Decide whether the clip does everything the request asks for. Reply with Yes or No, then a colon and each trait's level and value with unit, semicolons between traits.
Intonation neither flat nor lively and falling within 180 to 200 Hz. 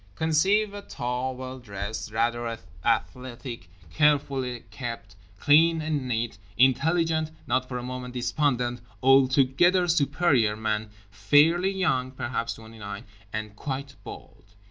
No: average, 4.2 semitones; low, 130 Hz